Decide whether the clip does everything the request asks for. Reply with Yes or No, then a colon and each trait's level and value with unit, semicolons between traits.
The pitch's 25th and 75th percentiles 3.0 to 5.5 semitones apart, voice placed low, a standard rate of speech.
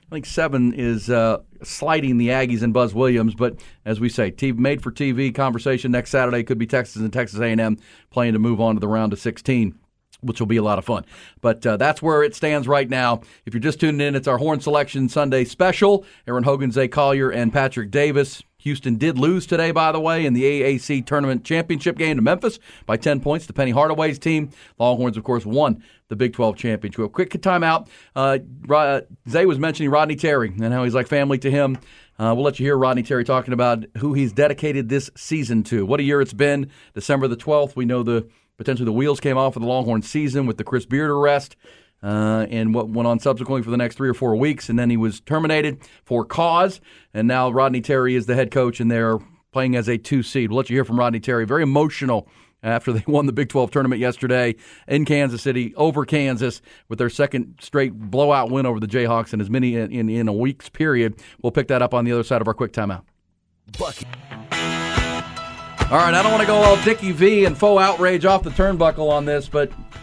No: average, 3.8 semitones; low, 130 Hz; fast, 225 wpm